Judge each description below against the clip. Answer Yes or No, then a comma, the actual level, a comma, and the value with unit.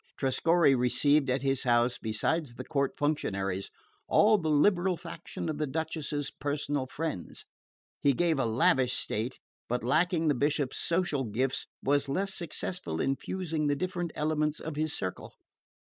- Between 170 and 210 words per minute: No, average, 150 wpm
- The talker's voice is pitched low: No, medium, 145 Hz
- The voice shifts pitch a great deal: No, average, 3.8 semitones